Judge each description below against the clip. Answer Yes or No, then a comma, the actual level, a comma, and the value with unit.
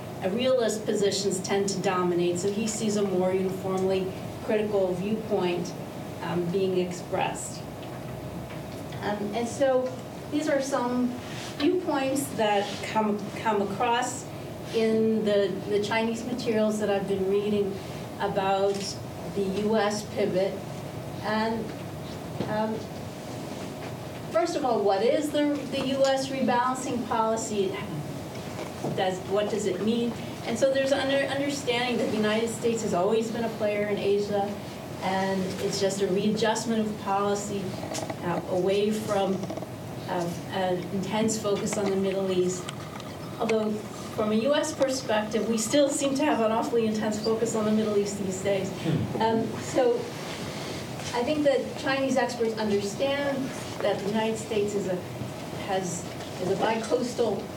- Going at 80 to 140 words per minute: Yes, slow, 135 wpm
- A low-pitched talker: No, high, 210 Hz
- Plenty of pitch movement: No, average, 3.2 semitones